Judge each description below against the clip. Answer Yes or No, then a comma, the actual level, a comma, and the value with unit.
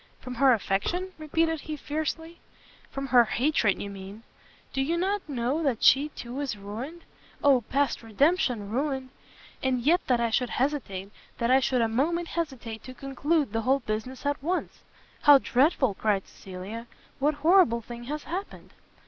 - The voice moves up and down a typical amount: Yes, average, 4.7 semitones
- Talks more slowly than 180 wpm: Yes, average, 165 wpm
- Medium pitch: No, very high, 265 Hz